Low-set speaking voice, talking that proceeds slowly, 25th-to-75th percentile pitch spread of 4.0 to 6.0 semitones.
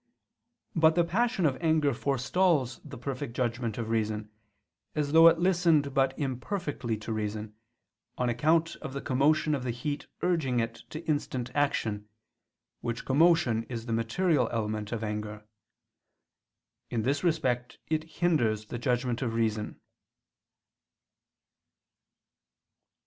Yes: low, 130 Hz; slow, 125 wpm; average, 5.3 semitones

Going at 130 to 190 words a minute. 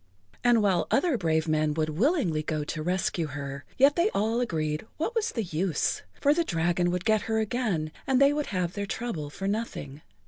No: average, 200 wpm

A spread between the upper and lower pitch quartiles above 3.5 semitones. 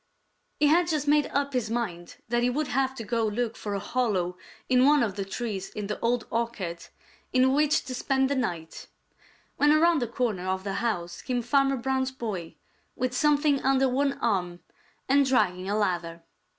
Yes: average, 5.2 semitones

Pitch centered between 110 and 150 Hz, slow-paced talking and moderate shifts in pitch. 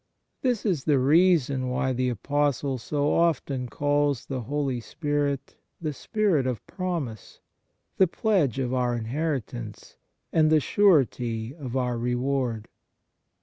Yes: medium, 140 Hz; slow, 130 wpm; average, 3.7 semitones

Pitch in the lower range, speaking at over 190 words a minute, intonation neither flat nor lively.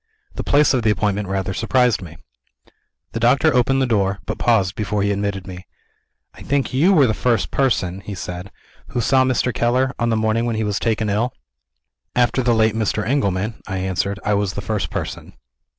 Yes: low, 110 Hz; average, 200 wpm; average, 3.9 semitones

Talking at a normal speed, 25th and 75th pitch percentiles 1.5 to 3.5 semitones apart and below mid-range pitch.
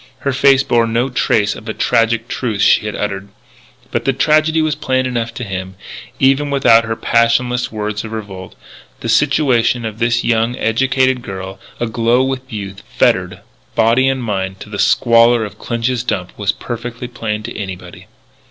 Yes: average, 170 wpm; average, 3.1 semitones; low, 115 Hz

